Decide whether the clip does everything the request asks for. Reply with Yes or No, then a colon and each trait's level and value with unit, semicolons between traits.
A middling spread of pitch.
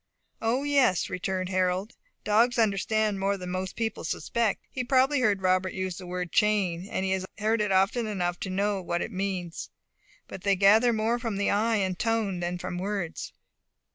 Yes: average, 3.2 semitones